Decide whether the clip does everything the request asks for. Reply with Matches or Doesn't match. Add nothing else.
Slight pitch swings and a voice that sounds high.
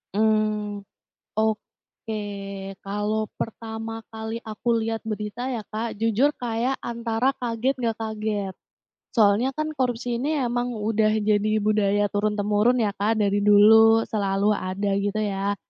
Matches